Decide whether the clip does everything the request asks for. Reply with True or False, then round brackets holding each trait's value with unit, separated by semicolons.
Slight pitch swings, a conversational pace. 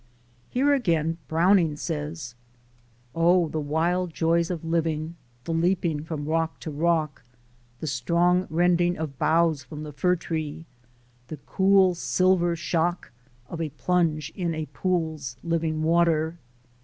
False (2.0 semitones; 130 wpm)